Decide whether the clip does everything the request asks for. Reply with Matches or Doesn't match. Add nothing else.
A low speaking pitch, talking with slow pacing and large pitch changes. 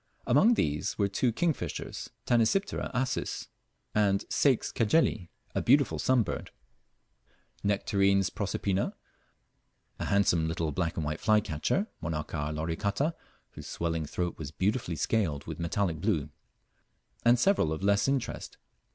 Matches